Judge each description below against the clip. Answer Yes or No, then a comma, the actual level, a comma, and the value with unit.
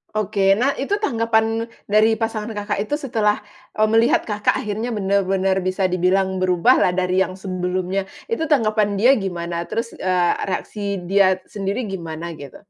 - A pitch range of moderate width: Yes, average, 3.1 semitones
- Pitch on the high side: Yes, high, 200 Hz